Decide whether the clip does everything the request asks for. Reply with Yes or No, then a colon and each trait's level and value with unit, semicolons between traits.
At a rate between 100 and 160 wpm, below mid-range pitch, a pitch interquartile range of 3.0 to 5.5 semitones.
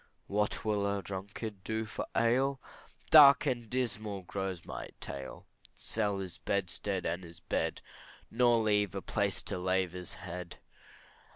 Yes: average, 145 wpm; low, 100 Hz; average, 3.4 semitones